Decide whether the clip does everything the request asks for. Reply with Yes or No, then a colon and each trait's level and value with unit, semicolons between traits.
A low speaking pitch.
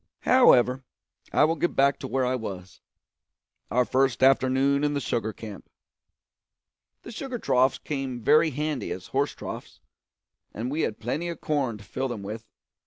Yes: low, 130 Hz